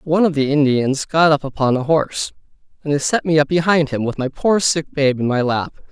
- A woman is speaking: No, male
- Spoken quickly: Yes, fast, 245 wpm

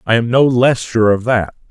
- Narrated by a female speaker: No, male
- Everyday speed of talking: No, fast, 245 wpm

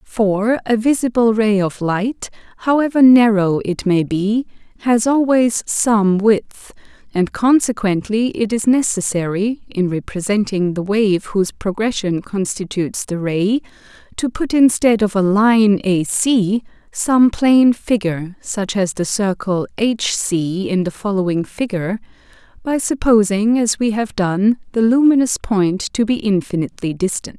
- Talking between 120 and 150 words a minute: Yes, average, 140 wpm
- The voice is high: Yes, high, 210 Hz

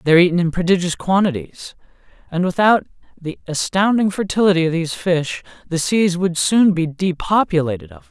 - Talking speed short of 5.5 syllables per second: No, 5.7 syllables/s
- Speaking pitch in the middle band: Yes, medium, 170 Hz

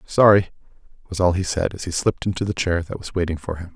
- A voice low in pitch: Yes, very low, 90 Hz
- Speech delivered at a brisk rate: Yes, fast, 255 wpm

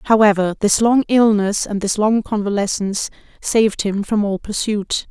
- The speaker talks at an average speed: Yes, average, 155 wpm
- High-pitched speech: Yes, high, 210 Hz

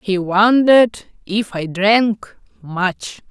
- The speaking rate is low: Yes, slow, 110 wpm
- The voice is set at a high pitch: Yes, high, 205 Hz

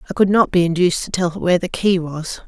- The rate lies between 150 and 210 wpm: No, fast, 265 wpm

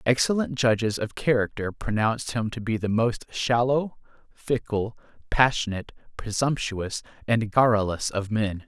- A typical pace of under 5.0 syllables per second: Yes, 4.6 syllables/s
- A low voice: Yes, low, 110 Hz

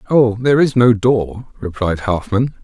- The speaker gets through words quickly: No, average, 160 wpm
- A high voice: No, low, 115 Hz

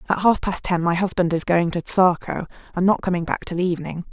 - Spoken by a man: No, female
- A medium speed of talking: No, fast, 235 wpm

